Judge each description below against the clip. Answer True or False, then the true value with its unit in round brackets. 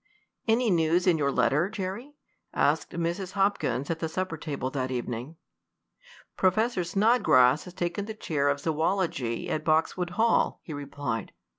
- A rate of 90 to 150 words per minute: True (145 wpm)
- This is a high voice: False (170 Hz)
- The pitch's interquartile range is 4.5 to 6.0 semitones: True (5.1 semitones)